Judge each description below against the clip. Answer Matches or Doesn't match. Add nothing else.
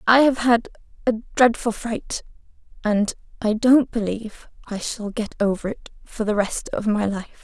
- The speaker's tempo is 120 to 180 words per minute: Matches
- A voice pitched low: Doesn't match